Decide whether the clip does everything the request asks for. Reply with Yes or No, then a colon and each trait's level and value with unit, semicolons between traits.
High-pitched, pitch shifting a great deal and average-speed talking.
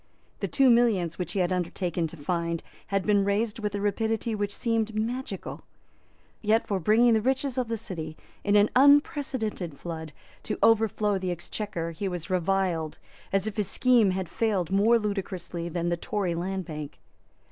No: high, 200 Hz; average, 4.3 semitones; average, 170 wpm